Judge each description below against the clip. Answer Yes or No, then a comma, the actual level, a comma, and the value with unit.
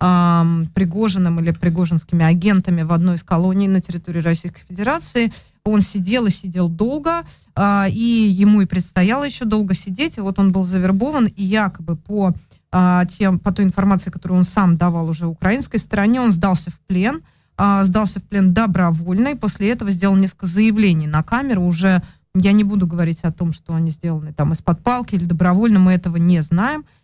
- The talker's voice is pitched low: No, high, 190 Hz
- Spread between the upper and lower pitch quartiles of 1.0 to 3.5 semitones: Yes, average, 3.1 semitones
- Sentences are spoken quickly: Yes, fast, 175 wpm